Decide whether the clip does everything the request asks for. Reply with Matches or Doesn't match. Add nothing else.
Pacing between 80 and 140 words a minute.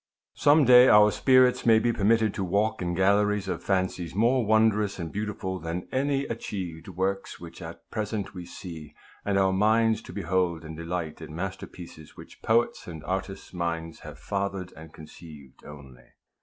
Doesn't match